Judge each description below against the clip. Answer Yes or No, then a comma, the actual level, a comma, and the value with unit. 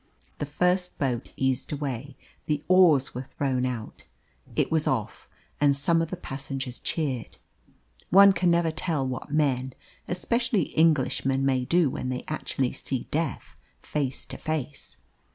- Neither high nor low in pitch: Yes, medium, 145 Hz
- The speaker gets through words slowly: No, average, 145 wpm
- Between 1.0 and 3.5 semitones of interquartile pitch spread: No, average, 3.9 semitones